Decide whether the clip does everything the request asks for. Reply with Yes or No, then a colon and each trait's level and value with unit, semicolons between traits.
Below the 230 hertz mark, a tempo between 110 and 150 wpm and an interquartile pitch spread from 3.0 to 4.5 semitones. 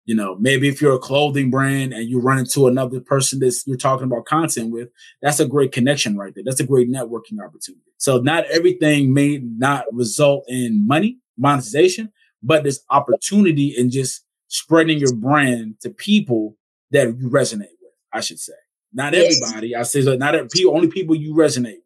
No: medium, 140 Hz; average, 190 wpm; average, 3.9 semitones